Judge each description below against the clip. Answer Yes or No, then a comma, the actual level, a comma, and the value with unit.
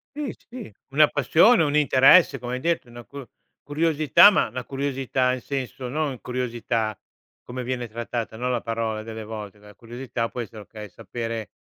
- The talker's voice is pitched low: Yes, low, 125 Hz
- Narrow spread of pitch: No, average, 3.6 semitones